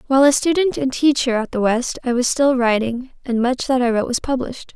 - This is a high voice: Yes, very high, 255 Hz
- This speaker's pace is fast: Yes, fast, 240 wpm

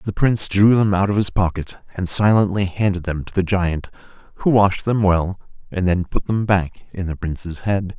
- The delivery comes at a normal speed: No, fast, 210 wpm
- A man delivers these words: Yes, male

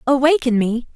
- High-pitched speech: Yes, very high, 260 Hz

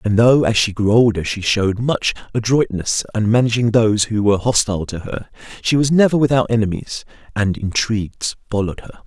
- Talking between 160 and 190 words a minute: Yes, average, 180 wpm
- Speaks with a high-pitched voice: No, low, 110 Hz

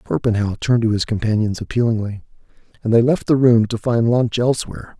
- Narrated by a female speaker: No, male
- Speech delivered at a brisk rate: No, average, 180 wpm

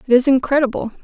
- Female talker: Yes, female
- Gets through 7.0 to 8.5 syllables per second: Yes, 7.4 syllables/s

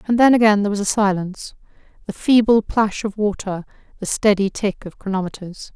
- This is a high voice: Yes, high, 205 Hz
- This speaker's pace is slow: No, average, 175 wpm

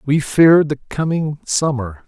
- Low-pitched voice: No, medium, 150 Hz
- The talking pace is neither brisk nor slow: Yes, average, 145 wpm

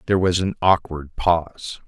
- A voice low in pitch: Yes, very low, 85 Hz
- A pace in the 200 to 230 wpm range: No, average, 160 wpm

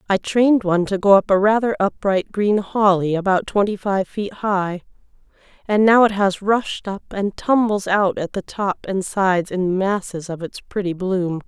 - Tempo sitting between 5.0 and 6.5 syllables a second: No, 4.6 syllables/s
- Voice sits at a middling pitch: No, high, 195 Hz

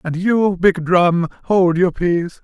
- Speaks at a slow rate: No, average, 170 wpm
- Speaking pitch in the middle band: Yes, medium, 180 Hz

